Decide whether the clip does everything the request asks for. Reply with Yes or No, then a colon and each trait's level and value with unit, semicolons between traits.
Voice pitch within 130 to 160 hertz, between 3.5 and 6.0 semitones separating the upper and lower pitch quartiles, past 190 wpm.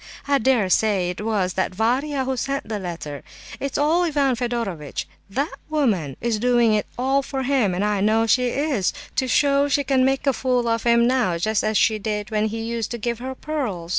No: high, 235 Hz; average, 4.3 semitones; fast, 205 wpm